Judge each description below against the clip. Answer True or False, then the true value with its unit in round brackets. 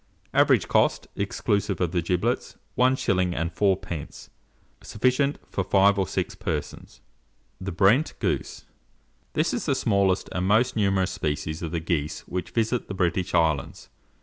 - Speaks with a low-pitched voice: True (95 Hz)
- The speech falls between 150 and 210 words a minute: False (140 wpm)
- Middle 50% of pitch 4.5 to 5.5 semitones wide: False (3.2 semitones)